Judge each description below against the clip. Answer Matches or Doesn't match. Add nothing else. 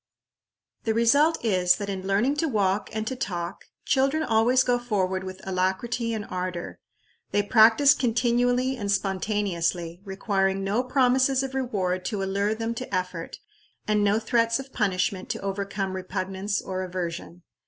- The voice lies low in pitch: Doesn't match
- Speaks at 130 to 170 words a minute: Matches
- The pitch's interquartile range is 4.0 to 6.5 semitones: Matches